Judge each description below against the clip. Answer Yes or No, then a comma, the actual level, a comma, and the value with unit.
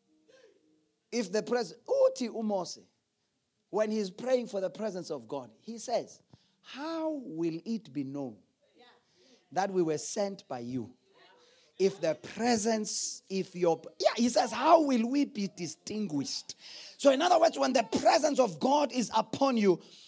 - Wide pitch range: Yes, wide, 7.5 semitones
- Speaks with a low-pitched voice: No, high, 220 Hz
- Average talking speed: Yes, average, 145 wpm